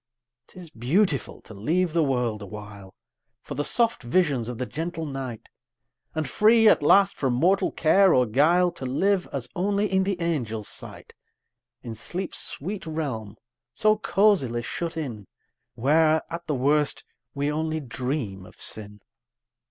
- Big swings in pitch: Yes, wide, 6.9 semitones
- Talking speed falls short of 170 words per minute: Yes, average, 150 wpm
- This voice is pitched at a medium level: Yes, medium, 150 Hz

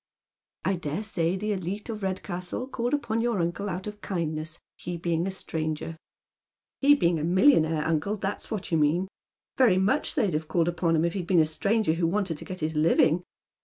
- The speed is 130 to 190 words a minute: No, fast, 205 wpm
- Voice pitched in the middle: Yes, medium, 180 Hz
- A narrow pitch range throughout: No, average, 4.0 semitones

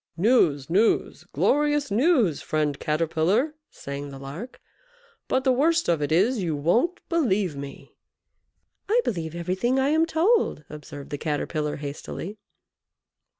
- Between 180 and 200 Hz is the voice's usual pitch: Yes, medium, 185 Hz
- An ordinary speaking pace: No, slow, 130 wpm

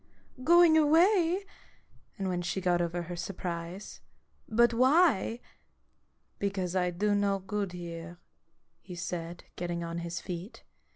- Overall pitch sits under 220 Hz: Yes, medium, 185 Hz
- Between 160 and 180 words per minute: No, average, 150 wpm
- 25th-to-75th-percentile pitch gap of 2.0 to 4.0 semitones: No, average, 5.1 semitones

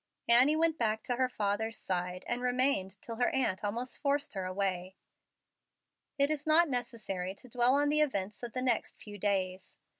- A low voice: No, high, 235 Hz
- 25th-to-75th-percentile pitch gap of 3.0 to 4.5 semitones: No, average, 5.1 semitones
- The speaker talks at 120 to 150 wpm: No, average, 180 wpm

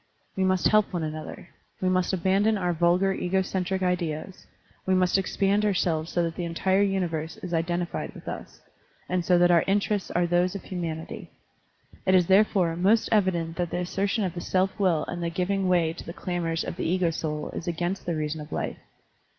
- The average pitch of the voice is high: No, medium, 180 Hz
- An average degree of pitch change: No, narrow, 2.1 semitones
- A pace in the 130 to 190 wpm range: No, average, 200 wpm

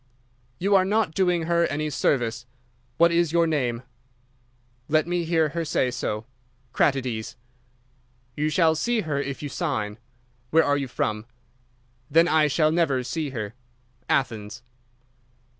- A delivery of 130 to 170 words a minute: Yes, average, 140 wpm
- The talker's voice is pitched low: No, medium, 150 Hz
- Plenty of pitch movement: No, average, 5.0 semitones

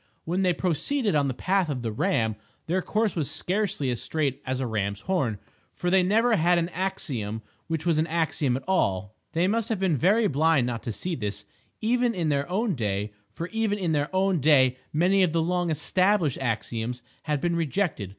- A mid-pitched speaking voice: Yes, medium, 165 Hz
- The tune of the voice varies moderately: No, wide, 6.6 semitones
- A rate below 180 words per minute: No, average, 200 wpm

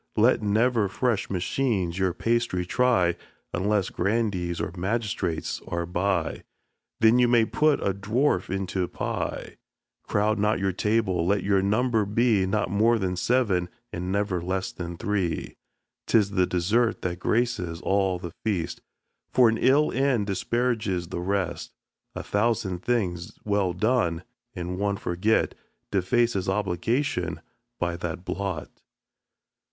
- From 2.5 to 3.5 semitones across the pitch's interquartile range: No, average, 4.0 semitones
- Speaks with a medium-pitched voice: No, low, 100 Hz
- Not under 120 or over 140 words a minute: Yes, slow, 135 wpm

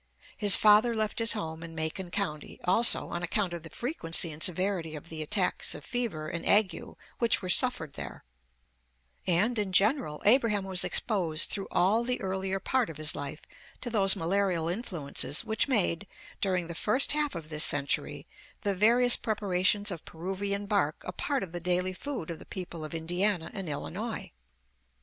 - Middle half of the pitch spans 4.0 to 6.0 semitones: Yes, average, 4.4 semitones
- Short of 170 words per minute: No, average, 175 wpm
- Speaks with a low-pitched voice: No, high, 190 Hz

